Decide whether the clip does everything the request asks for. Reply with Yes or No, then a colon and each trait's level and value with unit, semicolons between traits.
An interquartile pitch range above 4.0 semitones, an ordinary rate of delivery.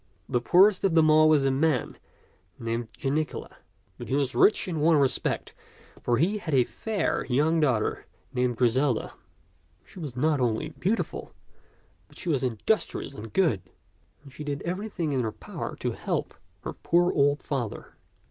Yes: average, 4.7 semitones; average, 165 wpm